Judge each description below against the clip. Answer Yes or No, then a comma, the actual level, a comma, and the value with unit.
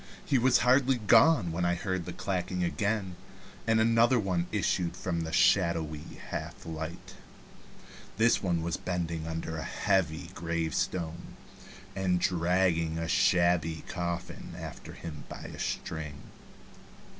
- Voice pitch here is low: Yes, very low, 90 Hz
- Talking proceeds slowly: Yes, slow, 130 wpm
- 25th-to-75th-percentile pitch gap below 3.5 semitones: Yes, average, 2.9 semitones